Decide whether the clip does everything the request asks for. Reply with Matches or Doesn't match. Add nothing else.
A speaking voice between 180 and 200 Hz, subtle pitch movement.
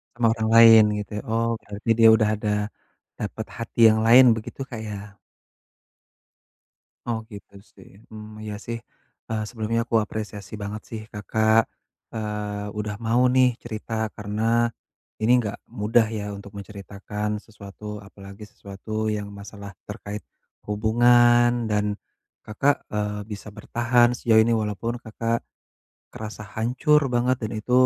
Doesn't match